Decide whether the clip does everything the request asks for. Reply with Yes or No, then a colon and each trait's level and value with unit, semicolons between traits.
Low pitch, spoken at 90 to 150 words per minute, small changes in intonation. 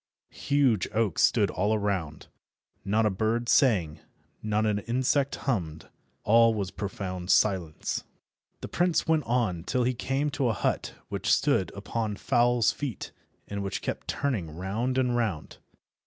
No: low, 110 Hz; average, 145 wpm; average, 4.5 semitones